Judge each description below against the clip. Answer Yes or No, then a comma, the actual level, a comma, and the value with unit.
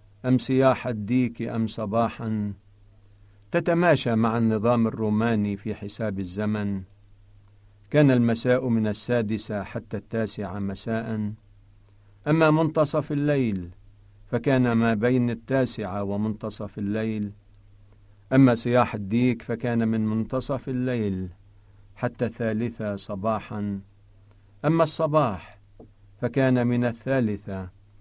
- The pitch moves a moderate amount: Yes, average, 3.3 semitones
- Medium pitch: No, low, 110 Hz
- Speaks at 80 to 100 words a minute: Yes, average, 90 wpm